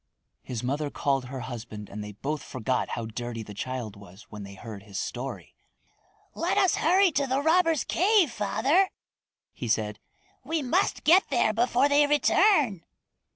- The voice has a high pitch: No, medium, 145 Hz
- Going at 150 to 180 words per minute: Yes, average, 160 wpm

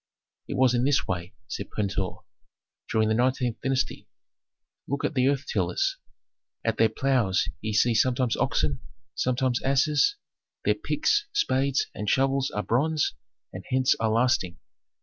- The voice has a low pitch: Yes, low, 125 Hz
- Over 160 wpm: No, average, 145 wpm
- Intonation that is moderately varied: Yes, average, 3.8 semitones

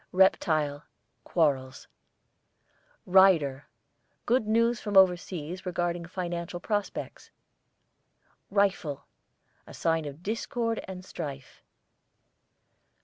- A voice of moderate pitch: Yes, medium, 175 Hz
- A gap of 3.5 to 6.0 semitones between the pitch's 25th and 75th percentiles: Yes, average, 4.0 semitones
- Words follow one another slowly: Yes, slow, 80 wpm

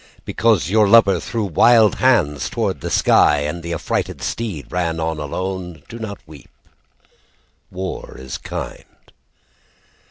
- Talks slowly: Yes, slow, 130 wpm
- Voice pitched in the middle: No, very low, 90 Hz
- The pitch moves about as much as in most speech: No, wide, 5.7 semitones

